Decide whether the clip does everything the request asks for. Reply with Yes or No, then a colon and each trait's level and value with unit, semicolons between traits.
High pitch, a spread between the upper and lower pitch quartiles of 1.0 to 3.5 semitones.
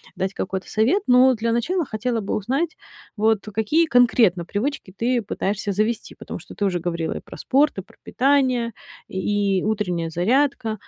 No: high, 220 Hz; average, 4.5 semitones